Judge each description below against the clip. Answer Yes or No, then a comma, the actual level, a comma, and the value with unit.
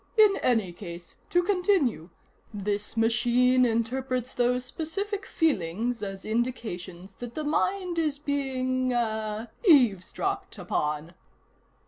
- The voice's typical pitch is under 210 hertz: No, high, 245 Hz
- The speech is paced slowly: Yes, slow, 105 wpm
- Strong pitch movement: Yes, wide, 5.9 semitones